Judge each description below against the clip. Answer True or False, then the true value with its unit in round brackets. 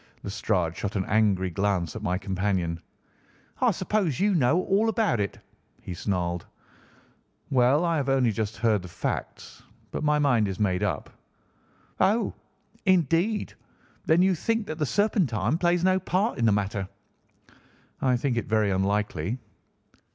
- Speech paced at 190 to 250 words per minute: False (150 wpm)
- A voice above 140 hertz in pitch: False (115 Hz)